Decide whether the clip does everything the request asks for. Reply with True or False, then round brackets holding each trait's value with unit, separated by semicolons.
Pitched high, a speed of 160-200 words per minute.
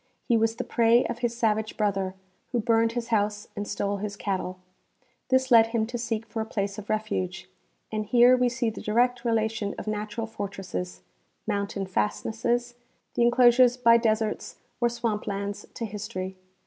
True (220 Hz; 170 wpm)